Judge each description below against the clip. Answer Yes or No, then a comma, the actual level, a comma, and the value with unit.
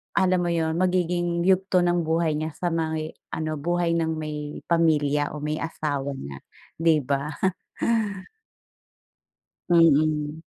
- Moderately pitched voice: Yes, medium, 160 Hz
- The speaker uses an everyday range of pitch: No, narrow, 2.3 semitones